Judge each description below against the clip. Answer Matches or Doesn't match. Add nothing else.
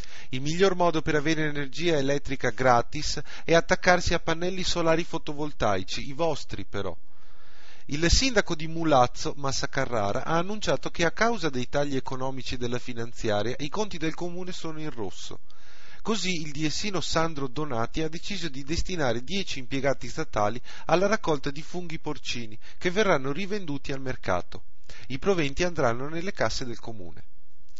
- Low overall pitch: Doesn't match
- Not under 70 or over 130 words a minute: Doesn't match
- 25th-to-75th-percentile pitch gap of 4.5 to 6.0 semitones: Matches